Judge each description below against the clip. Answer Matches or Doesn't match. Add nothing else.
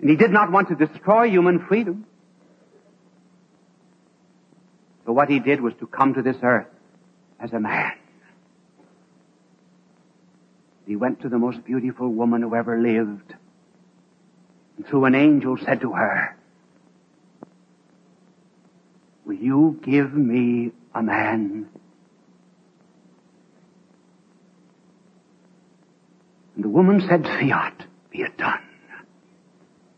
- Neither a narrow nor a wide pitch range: Doesn't match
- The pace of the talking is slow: Matches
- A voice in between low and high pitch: Doesn't match